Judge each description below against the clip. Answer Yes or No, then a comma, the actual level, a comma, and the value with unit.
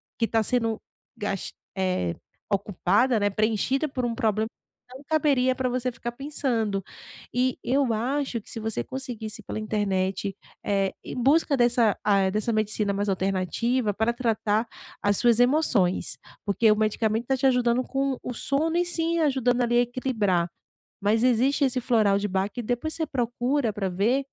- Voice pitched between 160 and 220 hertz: No, high, 230 Hz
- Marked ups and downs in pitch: No, average, 3.8 semitones